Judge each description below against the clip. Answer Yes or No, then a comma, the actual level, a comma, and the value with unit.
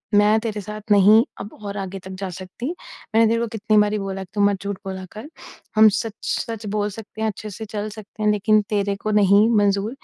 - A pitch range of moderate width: No, narrow, 1.5 semitones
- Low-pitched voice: No, high, 210 Hz